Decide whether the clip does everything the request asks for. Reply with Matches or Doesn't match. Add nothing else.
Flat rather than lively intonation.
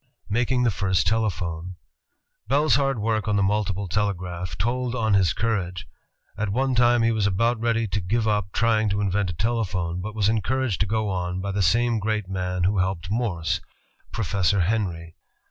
Doesn't match